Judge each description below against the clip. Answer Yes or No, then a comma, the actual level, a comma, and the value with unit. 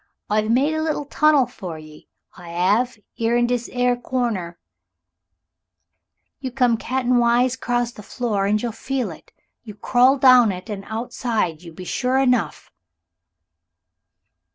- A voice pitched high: Yes, high, 240 Hz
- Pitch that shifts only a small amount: No, average, 3.7 semitones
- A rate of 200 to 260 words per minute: No, average, 150 wpm